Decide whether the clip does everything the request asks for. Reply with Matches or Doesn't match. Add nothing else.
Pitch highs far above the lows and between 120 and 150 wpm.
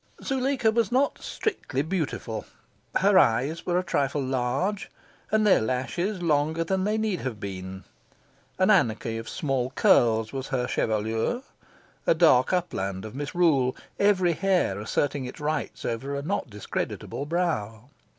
Matches